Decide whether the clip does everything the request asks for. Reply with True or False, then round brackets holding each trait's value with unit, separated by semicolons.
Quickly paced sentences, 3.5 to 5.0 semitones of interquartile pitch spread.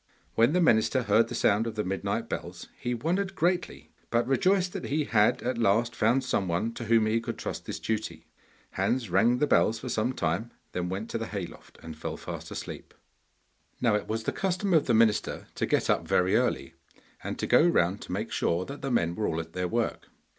True (220 wpm; 4.2 semitones)